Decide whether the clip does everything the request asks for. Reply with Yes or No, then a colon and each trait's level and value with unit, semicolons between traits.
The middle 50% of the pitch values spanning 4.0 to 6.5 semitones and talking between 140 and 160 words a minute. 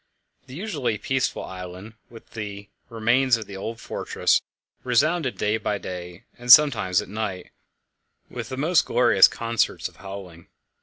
Yes: average, 4.8 semitones; average, 145 wpm